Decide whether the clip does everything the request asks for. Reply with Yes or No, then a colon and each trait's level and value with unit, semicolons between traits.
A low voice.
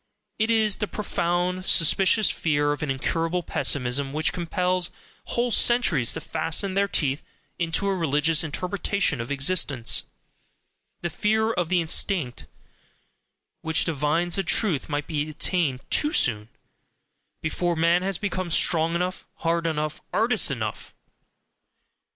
No: medium, 170 Hz